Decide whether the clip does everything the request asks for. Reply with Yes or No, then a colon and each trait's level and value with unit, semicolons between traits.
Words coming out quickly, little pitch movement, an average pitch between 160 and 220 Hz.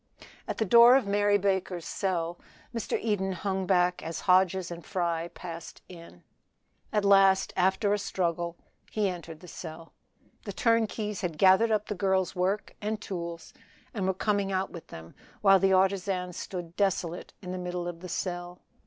No: average, 170 wpm; narrow, 2.3 semitones; medium, 185 Hz